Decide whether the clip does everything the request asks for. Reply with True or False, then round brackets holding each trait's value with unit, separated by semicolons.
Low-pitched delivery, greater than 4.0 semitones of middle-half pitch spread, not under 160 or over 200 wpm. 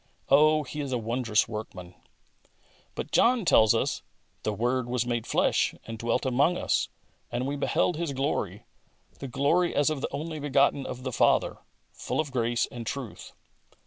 False (130 Hz; 3.7 semitones; 175 wpm)